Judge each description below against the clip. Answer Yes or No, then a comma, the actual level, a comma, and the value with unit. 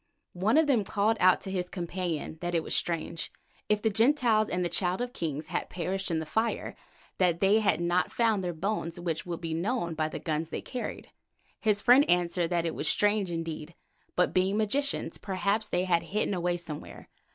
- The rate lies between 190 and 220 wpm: Yes, average, 195 wpm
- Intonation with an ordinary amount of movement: Yes, average, 3.8 semitones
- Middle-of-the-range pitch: Yes, medium, 180 Hz